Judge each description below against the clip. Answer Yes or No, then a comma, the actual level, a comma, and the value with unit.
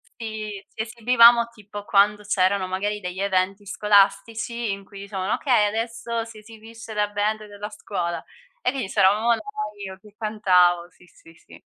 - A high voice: Yes, high, 210 Hz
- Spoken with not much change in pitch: Yes, narrow, 2.3 semitones